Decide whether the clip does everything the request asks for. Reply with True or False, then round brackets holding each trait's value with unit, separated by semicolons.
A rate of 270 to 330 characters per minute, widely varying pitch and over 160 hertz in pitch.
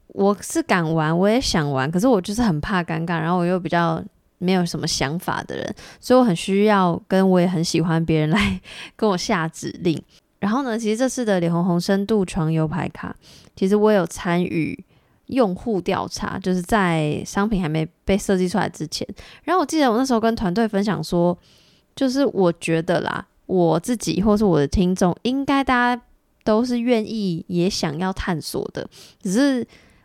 False (275 characters per minute; 4.4 semitones; 190 Hz)